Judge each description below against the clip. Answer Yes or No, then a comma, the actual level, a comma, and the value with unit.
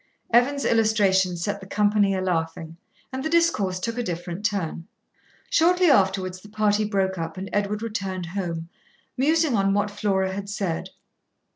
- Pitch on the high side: Yes, high, 200 Hz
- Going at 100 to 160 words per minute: Yes, average, 155 wpm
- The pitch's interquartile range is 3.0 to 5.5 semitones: No, narrow, 2.6 semitones